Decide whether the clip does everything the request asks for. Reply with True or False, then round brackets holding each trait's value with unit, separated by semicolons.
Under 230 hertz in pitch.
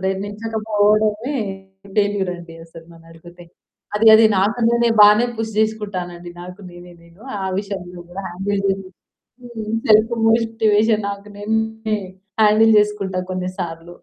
True (205 Hz)